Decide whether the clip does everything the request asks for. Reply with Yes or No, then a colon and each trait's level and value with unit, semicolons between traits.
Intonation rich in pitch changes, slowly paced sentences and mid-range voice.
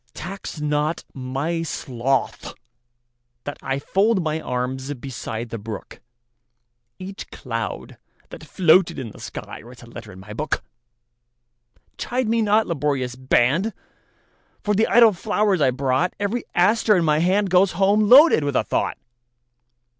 Yes: wide, 8.0 semitones; slow, 120 wpm; medium, 145 Hz